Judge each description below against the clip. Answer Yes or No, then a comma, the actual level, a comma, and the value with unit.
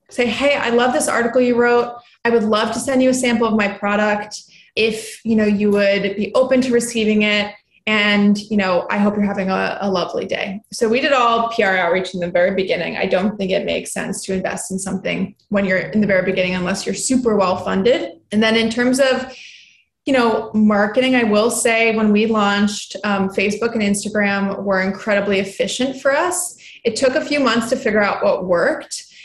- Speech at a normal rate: No, fast, 215 wpm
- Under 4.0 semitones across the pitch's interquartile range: Yes, average, 3.0 semitones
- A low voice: No, high, 210 Hz